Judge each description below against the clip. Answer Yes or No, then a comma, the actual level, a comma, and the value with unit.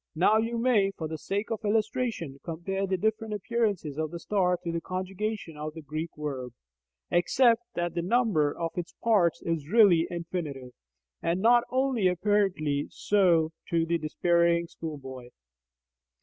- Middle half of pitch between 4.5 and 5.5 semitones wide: Yes, average, 4.8 semitones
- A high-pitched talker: No, medium, 175 Hz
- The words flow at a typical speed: Yes, average, 150 wpm